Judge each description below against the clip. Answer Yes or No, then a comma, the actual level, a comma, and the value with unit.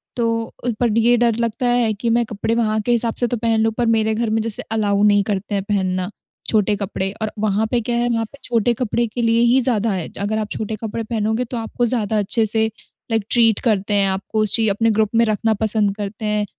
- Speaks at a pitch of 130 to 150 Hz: No, high, 220 Hz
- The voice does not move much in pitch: Yes, narrow, 1.9 semitones